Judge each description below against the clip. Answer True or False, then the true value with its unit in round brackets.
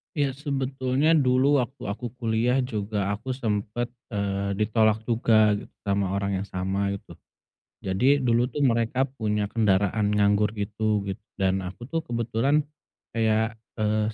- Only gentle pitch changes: False (3.7 semitones)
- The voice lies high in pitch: False (110 Hz)